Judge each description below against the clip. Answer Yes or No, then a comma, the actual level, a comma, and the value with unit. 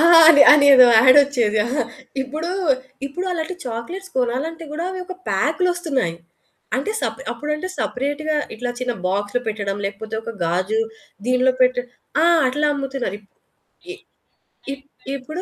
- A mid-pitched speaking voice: No, very high, 265 Hz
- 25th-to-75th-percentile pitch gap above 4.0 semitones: Yes, average, 4.8 semitones